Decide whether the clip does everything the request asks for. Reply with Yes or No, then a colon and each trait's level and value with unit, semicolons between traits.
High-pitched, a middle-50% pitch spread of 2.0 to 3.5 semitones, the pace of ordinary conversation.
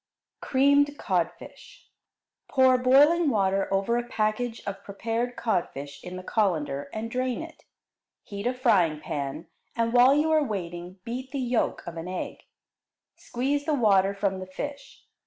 No: high, 225 Hz; wide, 5.6 semitones; average, 150 wpm